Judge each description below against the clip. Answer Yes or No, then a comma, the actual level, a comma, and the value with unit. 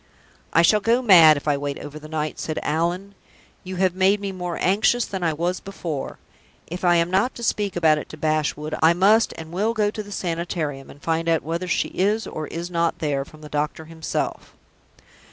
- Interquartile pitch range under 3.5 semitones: No, average, 3.8 semitones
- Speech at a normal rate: No, fast, 210 wpm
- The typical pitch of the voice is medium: Yes, medium, 170 Hz